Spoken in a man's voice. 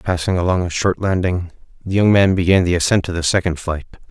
Yes: male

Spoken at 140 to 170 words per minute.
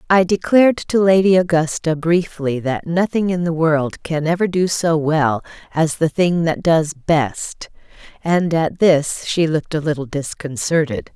Yes: average, 160 wpm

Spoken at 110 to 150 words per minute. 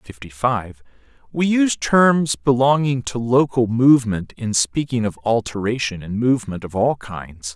Yes: average, 145 wpm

